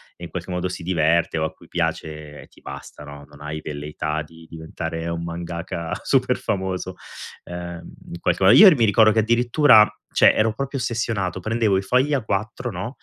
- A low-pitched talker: Yes, very low, 90 Hz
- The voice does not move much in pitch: No, average, 5.0 semitones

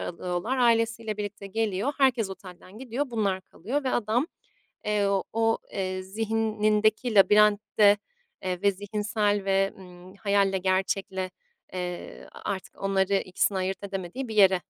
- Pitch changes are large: No, average, 2.7 semitones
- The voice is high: Yes, high, 205 Hz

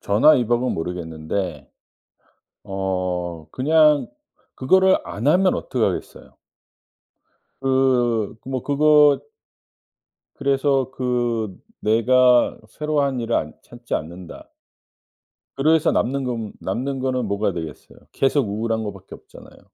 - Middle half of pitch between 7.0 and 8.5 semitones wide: No, wide, 5.4 semitones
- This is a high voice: No, low, 120 Hz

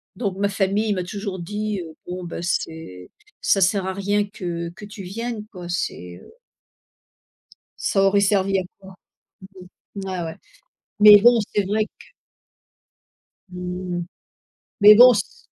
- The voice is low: No, high, 195 Hz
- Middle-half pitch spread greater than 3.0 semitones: No, narrow, 2.6 semitones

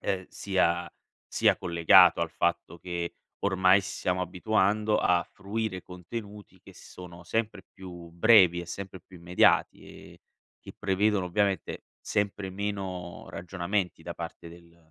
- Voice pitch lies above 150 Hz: No, very low, 90 Hz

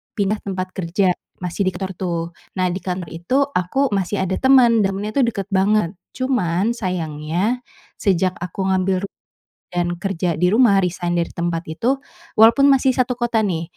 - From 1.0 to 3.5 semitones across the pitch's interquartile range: No, average, 4.2 semitones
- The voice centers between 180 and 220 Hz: Yes, high, 190 Hz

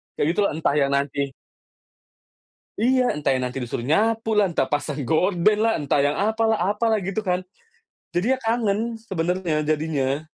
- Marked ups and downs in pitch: Yes, wide, 7.0 semitones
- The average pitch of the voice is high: No, medium, 180 Hz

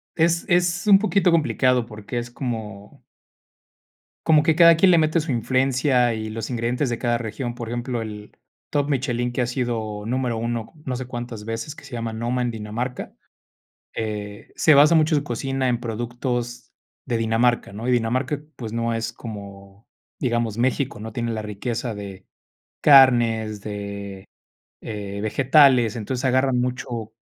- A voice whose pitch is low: Yes, low, 120 Hz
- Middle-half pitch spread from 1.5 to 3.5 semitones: Yes, average, 2.9 semitones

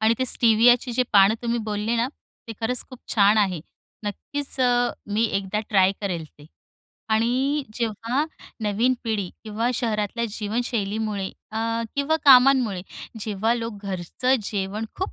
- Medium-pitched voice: No, high, 225 Hz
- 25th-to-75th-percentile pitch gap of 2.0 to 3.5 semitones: Yes, average, 3.0 semitones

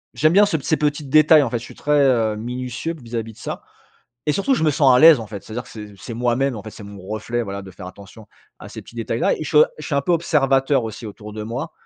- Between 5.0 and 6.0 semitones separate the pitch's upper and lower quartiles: Yes, average, 5.3 semitones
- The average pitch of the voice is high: No, low, 120 Hz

